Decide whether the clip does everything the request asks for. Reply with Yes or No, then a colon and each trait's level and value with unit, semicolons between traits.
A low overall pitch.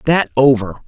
Yes: low, 130 Hz